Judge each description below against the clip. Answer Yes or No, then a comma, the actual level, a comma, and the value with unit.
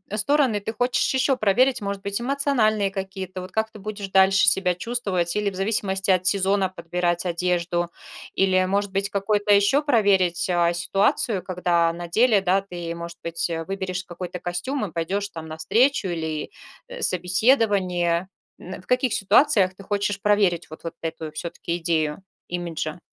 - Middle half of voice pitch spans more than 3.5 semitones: No, average, 2.9 semitones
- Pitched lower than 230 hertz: Yes, high, 190 Hz